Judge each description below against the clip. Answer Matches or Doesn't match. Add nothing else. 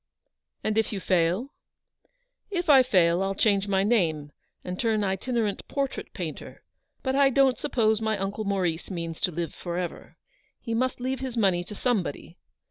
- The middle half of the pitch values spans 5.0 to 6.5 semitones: Matches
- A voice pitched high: Matches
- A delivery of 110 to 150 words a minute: Doesn't match